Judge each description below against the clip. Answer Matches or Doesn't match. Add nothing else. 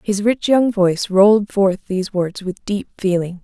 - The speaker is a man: Doesn't match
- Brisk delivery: Doesn't match